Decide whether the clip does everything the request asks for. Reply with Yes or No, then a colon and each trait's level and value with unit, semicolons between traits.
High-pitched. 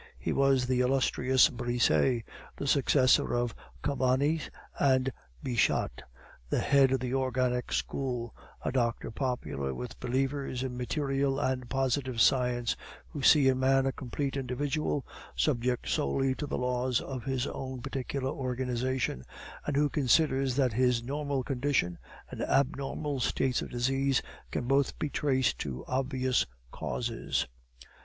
No: low, 130 Hz